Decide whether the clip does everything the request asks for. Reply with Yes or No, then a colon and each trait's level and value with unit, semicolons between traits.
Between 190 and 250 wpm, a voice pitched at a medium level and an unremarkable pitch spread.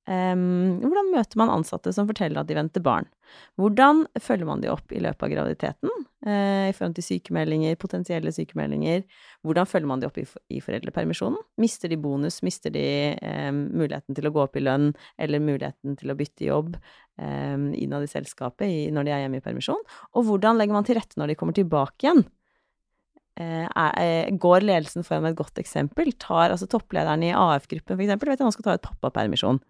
No: average, 200 wpm; medium, 170 Hz; wide, 5.8 semitones